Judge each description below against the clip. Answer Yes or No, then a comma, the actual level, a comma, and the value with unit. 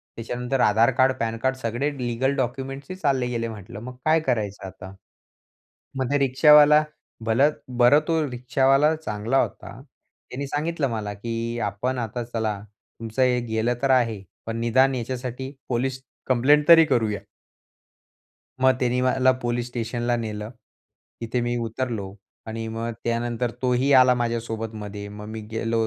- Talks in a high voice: No, low, 120 Hz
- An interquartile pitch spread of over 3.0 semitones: No, average, 2.7 semitones